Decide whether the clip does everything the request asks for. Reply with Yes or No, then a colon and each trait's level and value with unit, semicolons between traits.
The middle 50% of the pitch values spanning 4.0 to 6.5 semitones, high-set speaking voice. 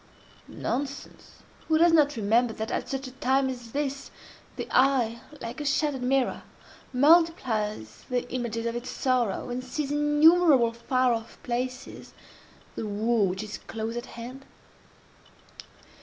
No: average, 3.2 semitones; very high, 250 Hz